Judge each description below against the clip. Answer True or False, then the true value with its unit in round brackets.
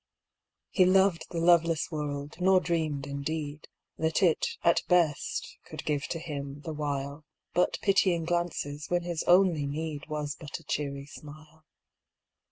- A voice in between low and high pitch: True (155 Hz)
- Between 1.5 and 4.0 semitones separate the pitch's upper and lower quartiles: True (3.0 semitones)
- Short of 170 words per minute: True (150 wpm)